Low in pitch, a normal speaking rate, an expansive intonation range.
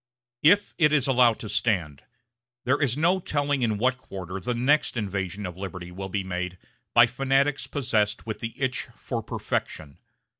Yes: low, 115 Hz; average, 165 wpm; wide, 6.0 semitones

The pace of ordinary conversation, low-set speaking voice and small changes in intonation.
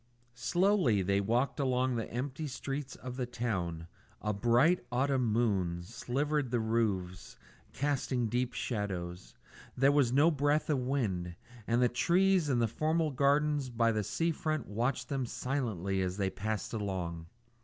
No: average, 150 wpm; low, 125 Hz; wide, 5.4 semitones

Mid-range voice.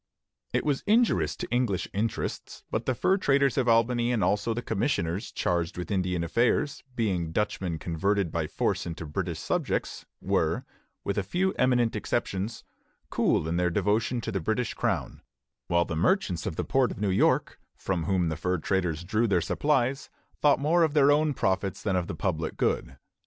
No: low, 100 Hz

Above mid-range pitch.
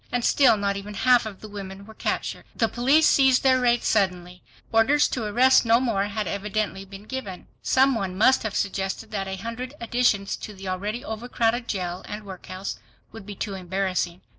Yes: high, 210 Hz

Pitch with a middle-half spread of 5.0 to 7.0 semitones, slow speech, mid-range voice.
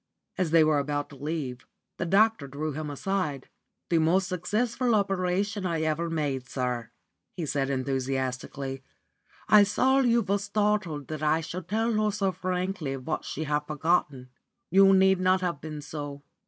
No: average, 5.3 semitones; average, 160 wpm; medium, 165 Hz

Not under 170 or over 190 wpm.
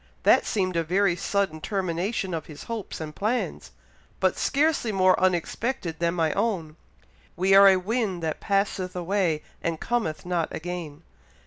No: average, 150 wpm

